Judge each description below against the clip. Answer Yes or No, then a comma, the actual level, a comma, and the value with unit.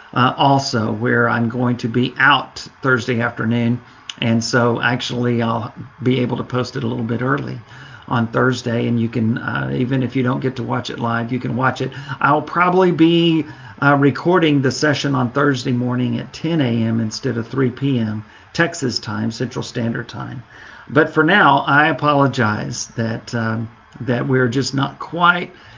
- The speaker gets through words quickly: No, average, 175 wpm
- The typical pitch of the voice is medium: No, low, 125 Hz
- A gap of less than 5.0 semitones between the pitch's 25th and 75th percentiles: Yes, average, 2.8 semitones